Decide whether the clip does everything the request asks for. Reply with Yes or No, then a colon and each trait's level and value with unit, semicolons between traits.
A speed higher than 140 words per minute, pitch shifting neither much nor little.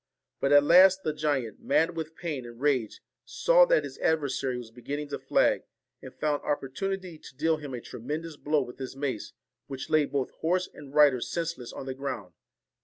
Yes: average, 185 wpm; average, 3.6 semitones